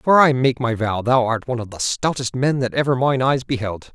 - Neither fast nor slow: No, fast, 260 wpm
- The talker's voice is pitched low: Yes, low, 125 Hz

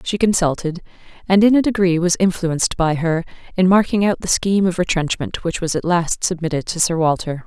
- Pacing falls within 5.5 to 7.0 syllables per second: Yes, 5.6 syllables/s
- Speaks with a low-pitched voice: No, medium, 175 Hz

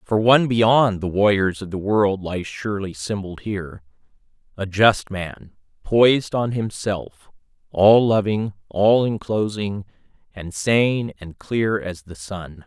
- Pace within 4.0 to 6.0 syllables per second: No, 3.8 syllables/s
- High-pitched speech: No, low, 100 Hz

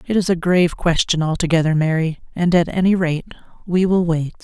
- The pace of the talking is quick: No, average, 190 wpm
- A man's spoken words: No, female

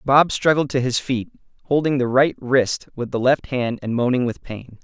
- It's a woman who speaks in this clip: No, male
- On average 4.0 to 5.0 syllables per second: Yes, 4.7 syllables/s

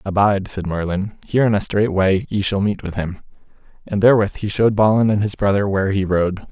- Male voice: Yes, male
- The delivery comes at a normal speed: No, fast, 220 wpm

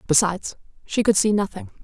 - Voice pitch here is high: Yes, high, 200 Hz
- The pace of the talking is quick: No, average, 165 wpm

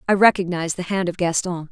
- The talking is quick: Yes, fast, 210 wpm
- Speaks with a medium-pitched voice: Yes, medium, 180 Hz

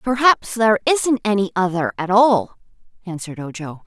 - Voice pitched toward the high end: Yes, high, 205 Hz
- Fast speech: No, average, 140 wpm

